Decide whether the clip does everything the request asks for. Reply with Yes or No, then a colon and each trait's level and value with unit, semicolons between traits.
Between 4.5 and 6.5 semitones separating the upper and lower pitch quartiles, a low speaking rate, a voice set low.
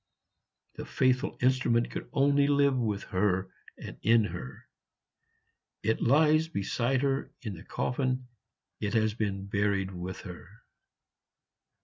Yes: average, 5.0 semitones; slow, 120 wpm; low, 115 Hz